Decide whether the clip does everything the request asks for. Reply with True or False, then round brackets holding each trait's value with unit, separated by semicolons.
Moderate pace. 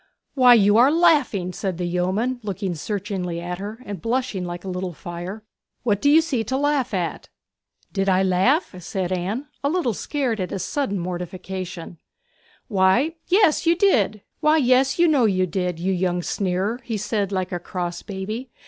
True (165 wpm)